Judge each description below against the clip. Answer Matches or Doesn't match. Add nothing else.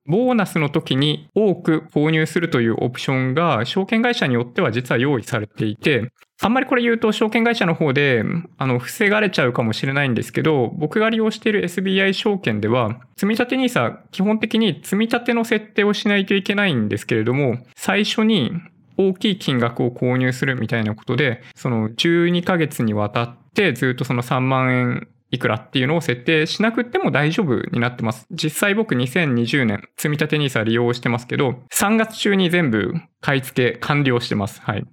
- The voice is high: Doesn't match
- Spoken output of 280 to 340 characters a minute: Doesn't match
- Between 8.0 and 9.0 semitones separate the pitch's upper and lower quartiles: Matches